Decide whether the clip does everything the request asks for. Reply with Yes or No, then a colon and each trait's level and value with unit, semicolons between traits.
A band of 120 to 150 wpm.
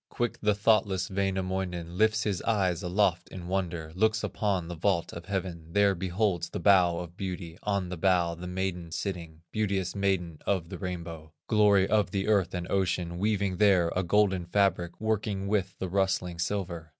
No: average, 175 wpm